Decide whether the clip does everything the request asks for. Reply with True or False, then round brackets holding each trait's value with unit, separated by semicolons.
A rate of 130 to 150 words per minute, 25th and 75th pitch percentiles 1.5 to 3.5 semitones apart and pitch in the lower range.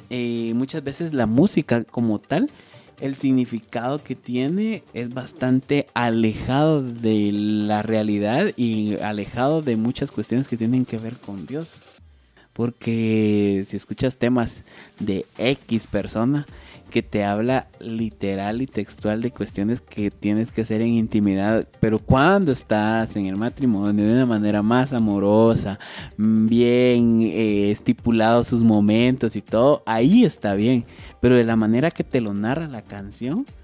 True (145 wpm; 3.2 semitones; 115 Hz)